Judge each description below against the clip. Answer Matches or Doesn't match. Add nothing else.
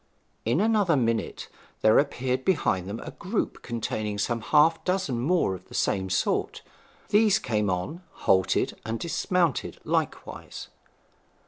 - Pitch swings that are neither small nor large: Doesn't match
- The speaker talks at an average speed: Doesn't match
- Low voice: Matches